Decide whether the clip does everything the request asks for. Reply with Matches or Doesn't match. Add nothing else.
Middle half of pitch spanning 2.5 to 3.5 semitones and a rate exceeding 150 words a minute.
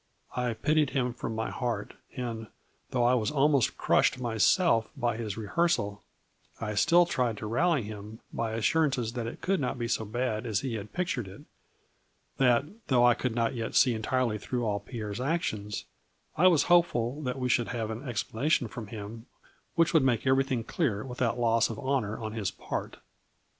Matches